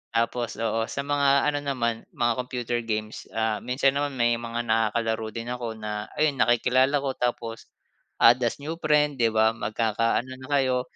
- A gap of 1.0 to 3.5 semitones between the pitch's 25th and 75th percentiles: Yes, average, 2.8 semitones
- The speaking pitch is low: Yes, low, 120 Hz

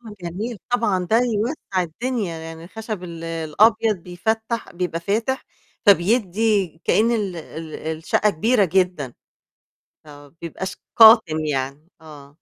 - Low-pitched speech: No, medium, 185 Hz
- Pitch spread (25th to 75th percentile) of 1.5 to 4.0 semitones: No, average, 5.3 semitones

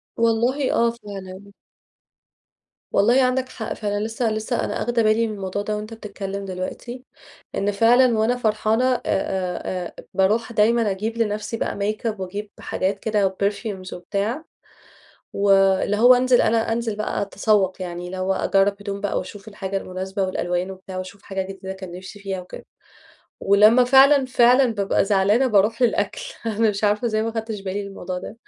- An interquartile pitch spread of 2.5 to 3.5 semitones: Yes, average, 2.9 semitones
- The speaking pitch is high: Yes, high, 205 Hz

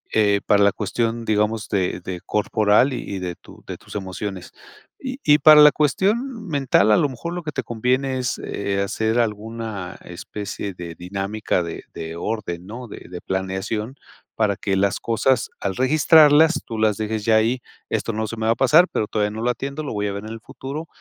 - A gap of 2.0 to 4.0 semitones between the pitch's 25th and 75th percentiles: No, average, 4.6 semitones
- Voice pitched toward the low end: Yes, low, 110 Hz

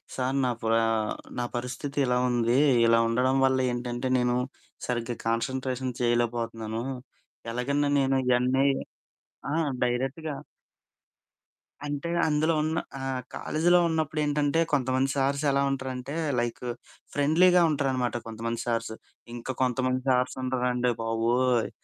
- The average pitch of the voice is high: No, low, 130 Hz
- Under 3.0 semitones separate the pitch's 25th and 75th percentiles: Yes, narrow, 2.5 semitones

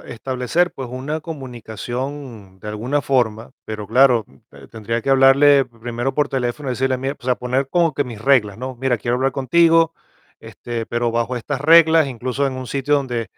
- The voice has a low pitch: Yes, low, 130 Hz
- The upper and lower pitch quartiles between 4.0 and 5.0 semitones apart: No, average, 2.8 semitones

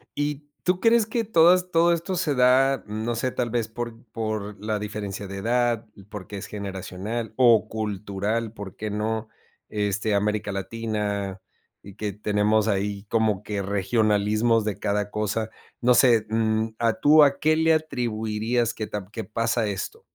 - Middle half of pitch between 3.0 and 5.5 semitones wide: No, narrow, 2.6 semitones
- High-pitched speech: No, low, 110 Hz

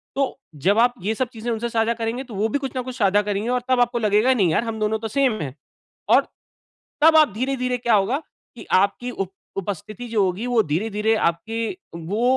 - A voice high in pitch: Yes, high, 225 Hz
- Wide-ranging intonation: No, average, 3.1 semitones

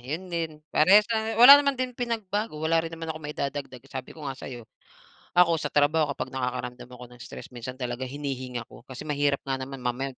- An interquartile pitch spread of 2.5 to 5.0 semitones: Yes, average, 4.5 semitones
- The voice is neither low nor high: Yes, medium, 145 Hz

